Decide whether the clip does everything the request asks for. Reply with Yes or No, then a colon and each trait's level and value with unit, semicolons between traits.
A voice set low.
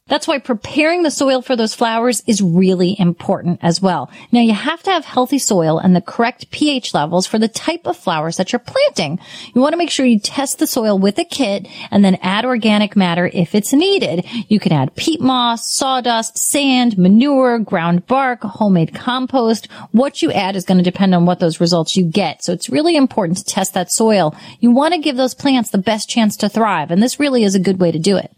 No: high, 220 Hz